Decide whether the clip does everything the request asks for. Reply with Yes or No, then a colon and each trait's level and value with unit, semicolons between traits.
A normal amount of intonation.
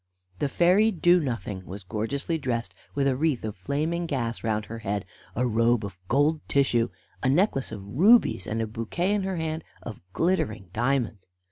No: wide, 6.6 semitones